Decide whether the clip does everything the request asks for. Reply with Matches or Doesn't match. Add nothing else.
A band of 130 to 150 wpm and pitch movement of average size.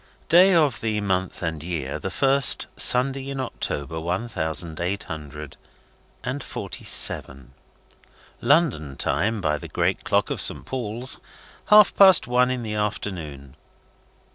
Doesn't match